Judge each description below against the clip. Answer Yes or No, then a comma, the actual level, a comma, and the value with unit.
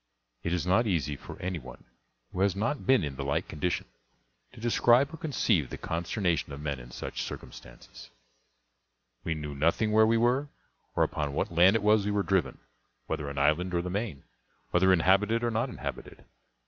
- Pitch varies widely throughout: Yes, wide, 6.6 semitones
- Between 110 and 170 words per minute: No, average, 185 wpm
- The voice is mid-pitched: No, very low, 90 Hz